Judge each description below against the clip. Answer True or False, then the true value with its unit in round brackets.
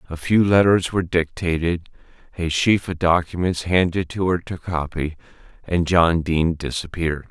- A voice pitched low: True (85 Hz)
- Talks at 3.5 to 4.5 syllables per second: False (4.9 syllables/s)